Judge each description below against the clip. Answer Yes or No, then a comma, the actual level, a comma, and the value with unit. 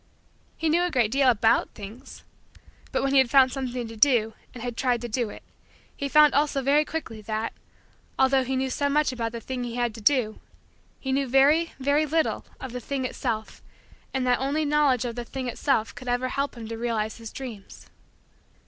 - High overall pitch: Yes, very high, 255 Hz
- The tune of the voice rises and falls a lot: No, average, 3.1 semitones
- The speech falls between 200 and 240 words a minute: Yes, fast, 205 wpm